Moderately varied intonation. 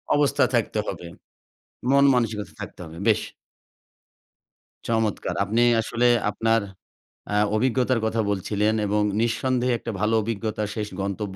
No: narrow, 2.2 semitones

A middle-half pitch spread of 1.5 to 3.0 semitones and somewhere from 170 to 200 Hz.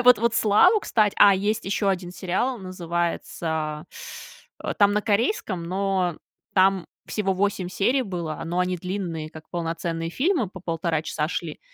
No: average, 3.4 semitones; medium, 185 Hz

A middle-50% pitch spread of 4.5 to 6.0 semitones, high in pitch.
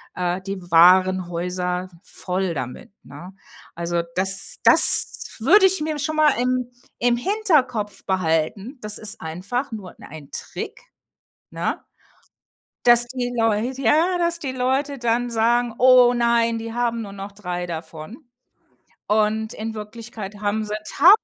Yes: average, 5.0 semitones; high, 220 Hz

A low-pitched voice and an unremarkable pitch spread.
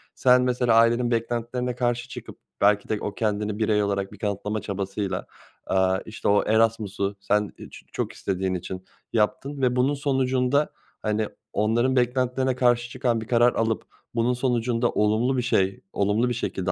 Yes: low, 115 Hz; average, 3.2 semitones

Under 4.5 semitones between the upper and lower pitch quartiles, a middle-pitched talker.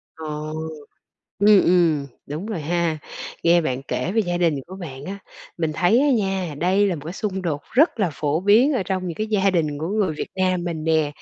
Yes: average, 3.8 semitones; medium, 175 Hz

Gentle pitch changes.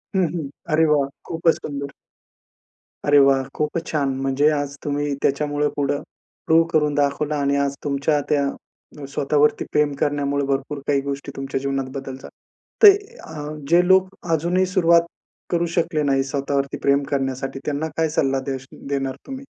Yes: narrow, 2.0 semitones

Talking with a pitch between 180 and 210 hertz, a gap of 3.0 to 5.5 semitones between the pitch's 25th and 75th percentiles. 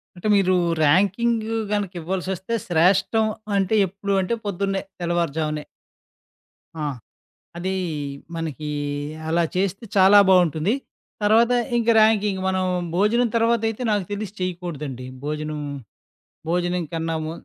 Yes: medium, 185 Hz; average, 3.5 semitones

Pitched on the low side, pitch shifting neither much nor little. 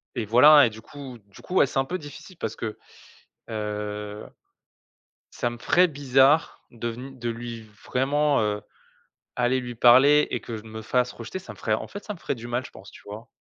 Yes: low, 120 Hz; average, 4.2 semitones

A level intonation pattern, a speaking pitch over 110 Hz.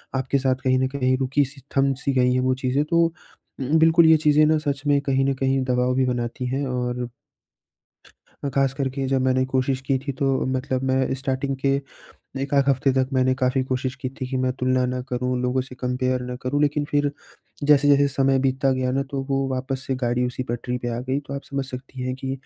Yes: narrow, 1.4 semitones; low, 130 Hz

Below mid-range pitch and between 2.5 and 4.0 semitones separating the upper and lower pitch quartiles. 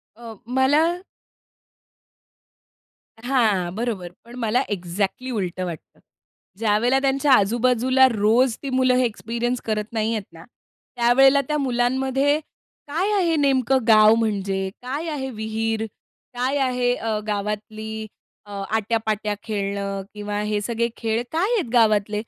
No: high, 230 Hz; average, 3.5 semitones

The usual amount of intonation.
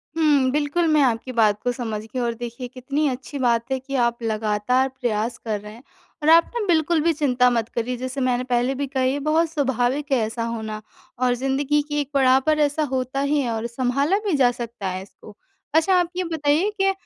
Yes: average, 3.7 semitones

